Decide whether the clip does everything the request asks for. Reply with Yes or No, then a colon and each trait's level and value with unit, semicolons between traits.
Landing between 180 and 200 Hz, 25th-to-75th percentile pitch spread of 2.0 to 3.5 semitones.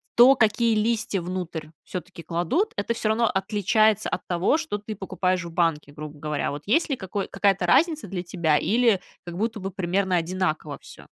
No: high, 190 Hz; average, 4.2 semitones